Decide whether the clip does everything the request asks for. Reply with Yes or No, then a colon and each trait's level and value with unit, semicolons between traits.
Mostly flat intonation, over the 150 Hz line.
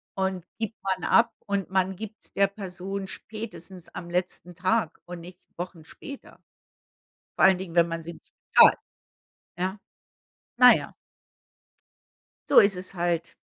Yes: narrow, 2.2 semitones; high, 190 Hz